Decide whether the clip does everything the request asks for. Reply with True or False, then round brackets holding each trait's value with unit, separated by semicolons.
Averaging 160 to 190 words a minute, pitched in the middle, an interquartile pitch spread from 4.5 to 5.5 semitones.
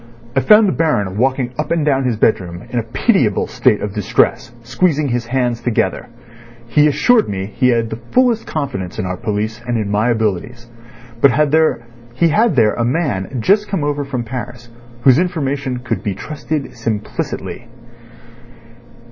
False (165 wpm; 125 Hz; 5.1 semitones)